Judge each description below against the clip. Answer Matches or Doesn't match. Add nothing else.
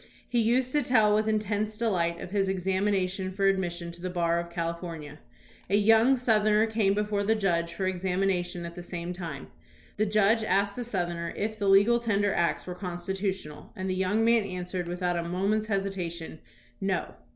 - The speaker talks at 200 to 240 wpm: Doesn't match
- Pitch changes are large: Doesn't match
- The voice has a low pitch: Doesn't match